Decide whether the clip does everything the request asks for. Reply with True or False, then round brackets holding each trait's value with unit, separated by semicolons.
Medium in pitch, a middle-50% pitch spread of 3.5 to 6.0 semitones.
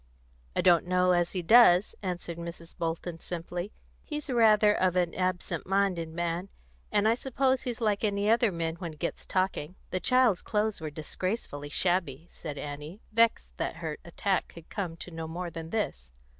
True (180 Hz; 3.9 semitones)